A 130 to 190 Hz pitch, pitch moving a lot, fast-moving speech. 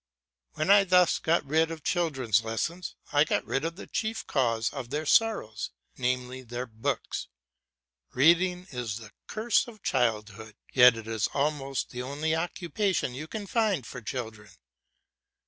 No: medium, 140 Hz; wide, 6.5 semitones; average, 150 wpm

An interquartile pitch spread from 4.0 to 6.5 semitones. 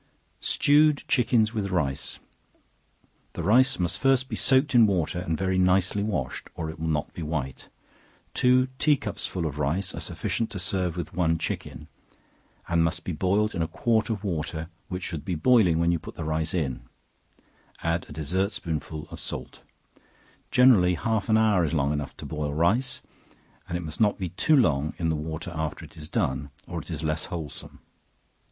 Yes: average, 5.2 semitones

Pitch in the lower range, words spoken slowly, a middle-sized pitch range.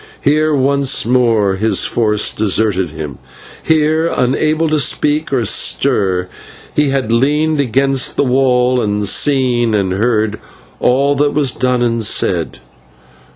Yes: low, 125 Hz; slow, 130 wpm; average, 4.7 semitones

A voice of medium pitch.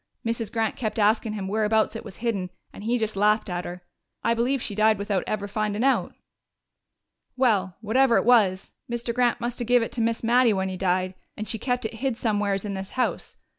No: high, 220 Hz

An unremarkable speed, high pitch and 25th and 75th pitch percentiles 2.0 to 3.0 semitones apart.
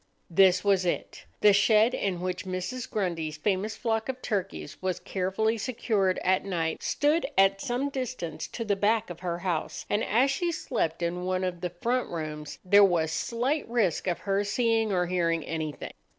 No: average, 180 wpm; high, 195 Hz; average, 4.2 semitones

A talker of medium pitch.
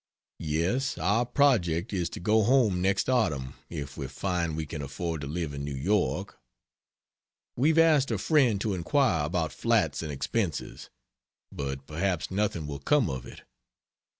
No: very low, 90 Hz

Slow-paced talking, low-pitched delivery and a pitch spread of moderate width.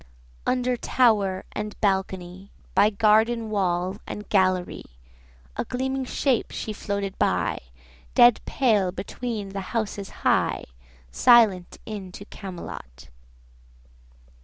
No: slow, 105 wpm; high, 205 Hz; average, 3.4 semitones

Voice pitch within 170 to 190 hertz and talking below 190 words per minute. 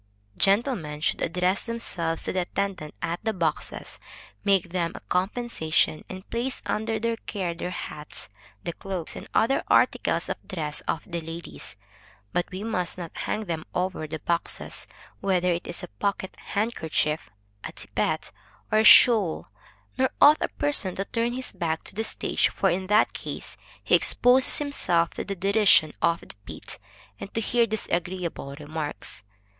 Yes: medium, 185 Hz; average, 165 wpm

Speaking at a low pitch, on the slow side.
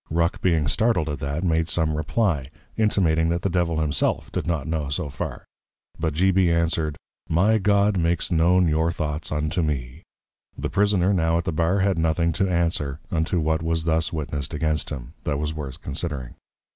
No: very low, 80 Hz; average, 185 wpm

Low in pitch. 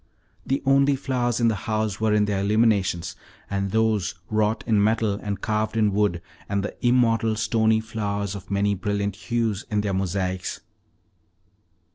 Yes: low, 105 Hz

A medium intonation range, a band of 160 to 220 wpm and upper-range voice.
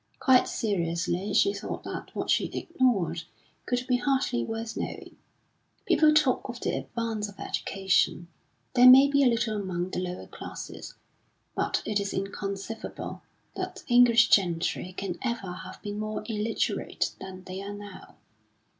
No: average, 4.5 semitones; average, 150 wpm; high, 210 Hz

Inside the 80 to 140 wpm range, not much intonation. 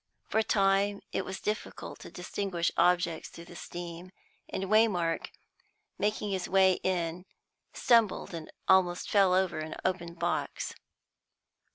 Yes: slow, 135 wpm; narrow, 2.3 semitones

